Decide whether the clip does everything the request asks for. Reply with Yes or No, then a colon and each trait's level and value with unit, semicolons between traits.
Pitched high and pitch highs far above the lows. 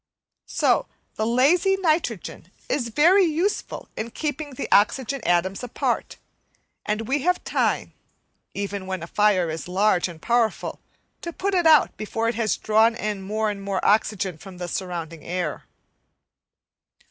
Yes: high, 215 Hz; wide, 6.7 semitones